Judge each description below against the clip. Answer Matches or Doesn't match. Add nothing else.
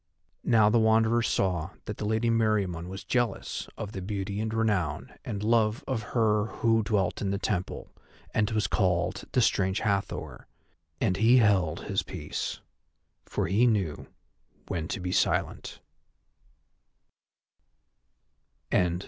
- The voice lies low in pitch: Matches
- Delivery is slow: Matches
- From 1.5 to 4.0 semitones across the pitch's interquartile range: Matches